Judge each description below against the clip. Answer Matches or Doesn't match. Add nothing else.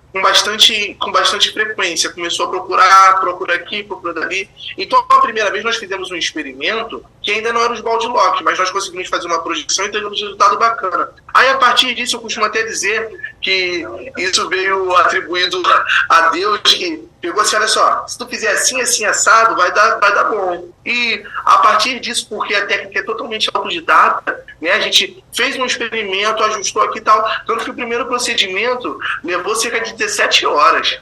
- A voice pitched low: Doesn't match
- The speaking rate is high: Matches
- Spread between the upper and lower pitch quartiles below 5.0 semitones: Matches